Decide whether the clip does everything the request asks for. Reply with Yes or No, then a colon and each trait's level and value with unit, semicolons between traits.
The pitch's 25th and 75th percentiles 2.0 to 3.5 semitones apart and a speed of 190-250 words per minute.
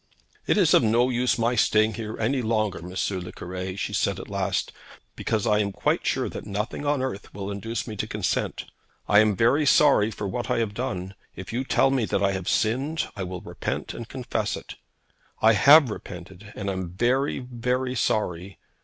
No: average, 4.2 semitones; average, 200 wpm